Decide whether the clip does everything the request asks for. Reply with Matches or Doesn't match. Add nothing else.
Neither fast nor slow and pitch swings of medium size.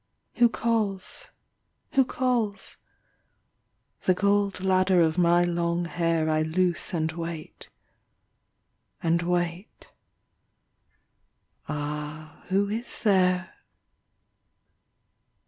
Doesn't match